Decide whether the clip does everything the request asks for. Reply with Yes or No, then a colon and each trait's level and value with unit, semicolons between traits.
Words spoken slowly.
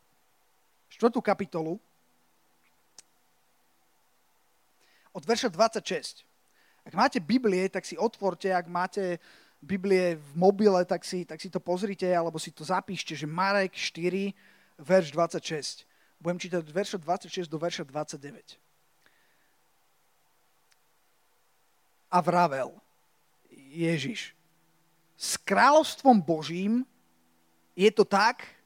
Yes: slow, 100 wpm